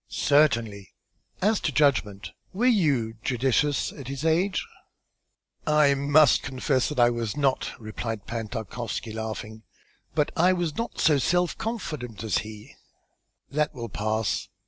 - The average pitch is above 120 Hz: Yes, low, 135 Hz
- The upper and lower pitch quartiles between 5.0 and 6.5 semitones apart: Yes, average, 5.3 semitones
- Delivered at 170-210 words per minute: No, slow, 135 wpm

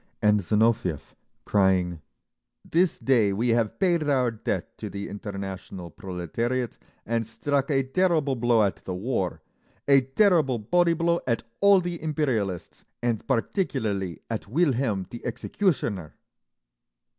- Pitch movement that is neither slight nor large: No, wide, 6.1 semitones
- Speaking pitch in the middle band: No, low, 115 Hz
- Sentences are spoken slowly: Yes, slow, 125 wpm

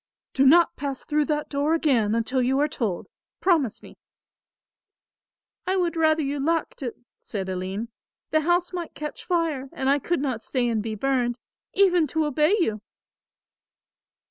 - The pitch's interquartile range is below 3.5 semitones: No, average, 4.9 semitones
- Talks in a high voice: Yes, very high, 285 Hz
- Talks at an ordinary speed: Yes, average, 160 wpm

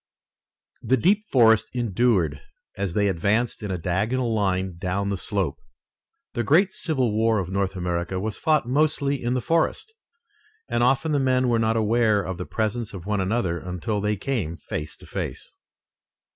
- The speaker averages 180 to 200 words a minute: No, average, 170 wpm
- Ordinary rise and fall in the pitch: Yes, average, 4.9 semitones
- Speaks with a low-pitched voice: Yes, low, 110 Hz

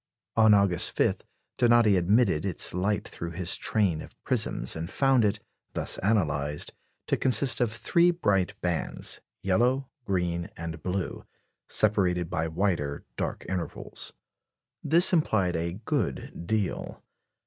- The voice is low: Yes, very low, 95 Hz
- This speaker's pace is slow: Yes, slow, 125 wpm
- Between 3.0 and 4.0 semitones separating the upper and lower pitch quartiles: No, average, 4.5 semitones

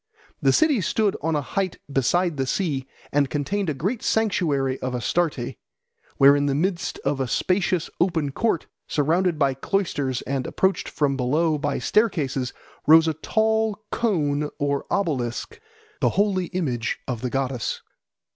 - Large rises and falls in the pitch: Yes, wide, 5.7 semitones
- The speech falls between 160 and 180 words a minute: No, average, 150 wpm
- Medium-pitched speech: Yes, medium, 155 Hz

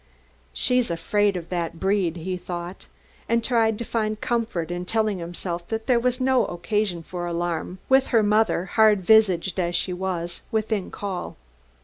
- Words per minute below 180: Yes, average, 160 wpm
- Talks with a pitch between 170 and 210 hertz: Yes, high, 190 Hz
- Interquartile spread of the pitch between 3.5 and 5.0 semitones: Yes, average, 4.1 semitones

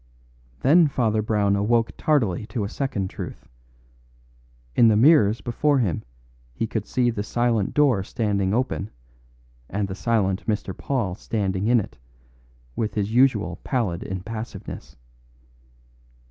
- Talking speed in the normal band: No, slow, 130 wpm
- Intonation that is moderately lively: Yes, average, 3.4 semitones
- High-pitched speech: No, low, 110 Hz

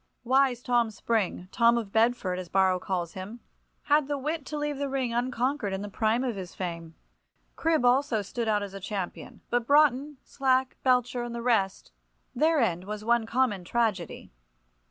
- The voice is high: Yes, high, 235 Hz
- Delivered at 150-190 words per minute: Yes, average, 165 wpm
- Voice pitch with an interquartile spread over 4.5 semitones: Yes, average, 5.1 semitones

